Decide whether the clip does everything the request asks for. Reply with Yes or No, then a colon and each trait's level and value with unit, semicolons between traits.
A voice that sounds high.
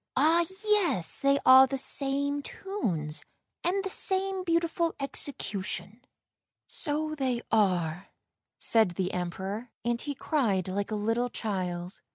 Yes: very high, 250 Hz